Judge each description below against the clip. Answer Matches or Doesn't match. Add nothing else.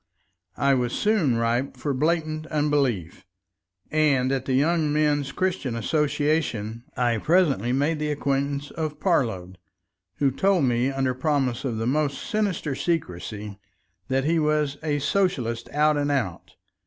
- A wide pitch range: Doesn't match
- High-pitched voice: Doesn't match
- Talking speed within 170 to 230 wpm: Doesn't match